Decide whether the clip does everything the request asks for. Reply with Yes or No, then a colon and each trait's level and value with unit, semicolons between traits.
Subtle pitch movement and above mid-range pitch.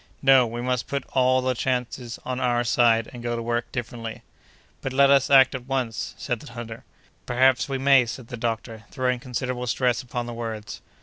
No: narrow, 1.7 semitones; low, 125 Hz